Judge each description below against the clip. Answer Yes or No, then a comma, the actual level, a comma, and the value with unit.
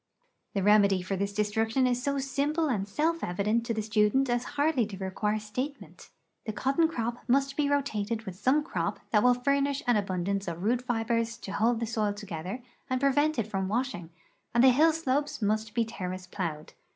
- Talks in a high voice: Yes, high, 230 Hz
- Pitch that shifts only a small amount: No, average, 4.8 semitones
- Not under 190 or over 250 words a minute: Yes, average, 195 wpm